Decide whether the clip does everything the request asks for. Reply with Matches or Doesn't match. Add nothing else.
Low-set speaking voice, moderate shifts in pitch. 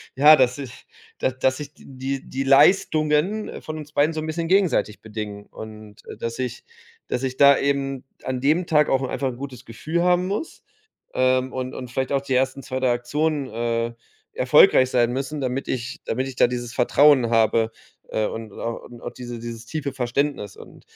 Matches